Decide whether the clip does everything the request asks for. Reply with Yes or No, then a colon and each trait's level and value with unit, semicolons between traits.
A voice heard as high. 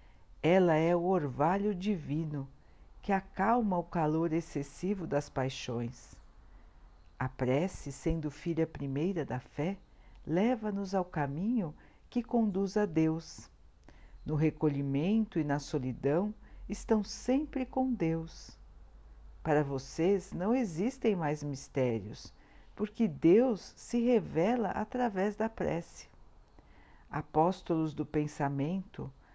No: medium, 160 Hz